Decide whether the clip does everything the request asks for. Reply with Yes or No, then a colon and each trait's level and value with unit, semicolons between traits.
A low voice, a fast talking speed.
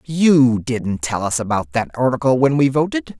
No: low, 130 Hz; average, 190 wpm